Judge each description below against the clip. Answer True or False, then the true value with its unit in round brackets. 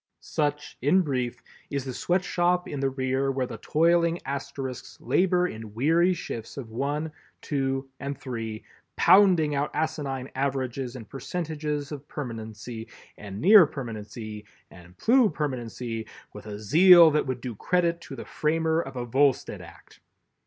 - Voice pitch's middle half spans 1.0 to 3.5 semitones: False (4.7 semitones)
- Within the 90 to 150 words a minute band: True (145 wpm)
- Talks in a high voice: False (140 Hz)